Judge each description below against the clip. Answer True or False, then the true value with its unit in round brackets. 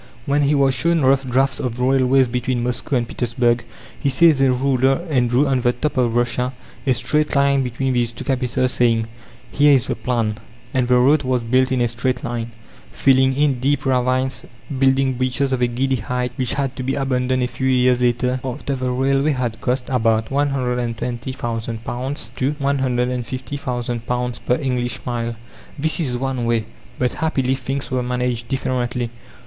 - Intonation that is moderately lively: False (1.7 semitones)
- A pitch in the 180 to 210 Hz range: False (130 Hz)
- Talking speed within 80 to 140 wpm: False (175 wpm)